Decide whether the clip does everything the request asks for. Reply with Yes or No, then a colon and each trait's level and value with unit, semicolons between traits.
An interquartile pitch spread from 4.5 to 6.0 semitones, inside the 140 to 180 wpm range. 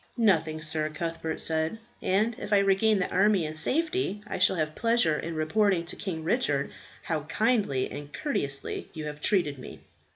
Yes: average, 5.2 semitones; average, 170 wpm